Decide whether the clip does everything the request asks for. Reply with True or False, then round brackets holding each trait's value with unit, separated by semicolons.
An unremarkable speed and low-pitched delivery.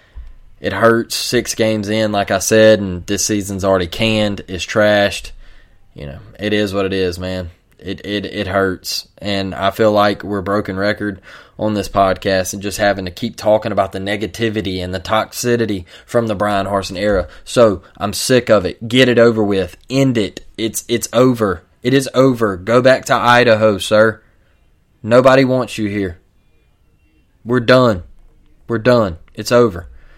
True (170 wpm; 105 Hz)